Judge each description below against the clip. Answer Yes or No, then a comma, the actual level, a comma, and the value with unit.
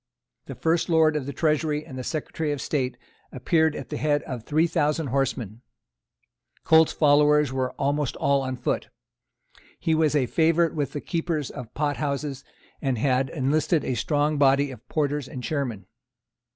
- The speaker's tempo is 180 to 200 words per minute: No, average, 165 wpm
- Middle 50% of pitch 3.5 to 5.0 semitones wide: No, average, 2.7 semitones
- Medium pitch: Yes, medium, 145 Hz